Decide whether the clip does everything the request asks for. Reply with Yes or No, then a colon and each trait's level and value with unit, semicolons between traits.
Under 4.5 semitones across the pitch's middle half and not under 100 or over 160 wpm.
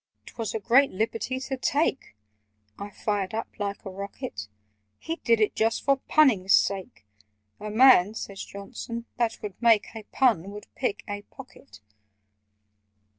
Yes: average, 3.7 semitones; average, 145 wpm